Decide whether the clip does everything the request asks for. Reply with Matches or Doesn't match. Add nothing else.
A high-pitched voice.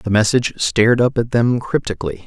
Doesn't match